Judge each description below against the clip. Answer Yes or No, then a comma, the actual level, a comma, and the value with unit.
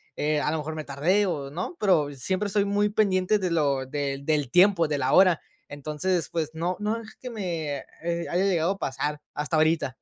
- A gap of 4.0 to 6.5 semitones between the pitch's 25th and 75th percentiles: Yes, average, 4.5 semitones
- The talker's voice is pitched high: No, medium, 165 Hz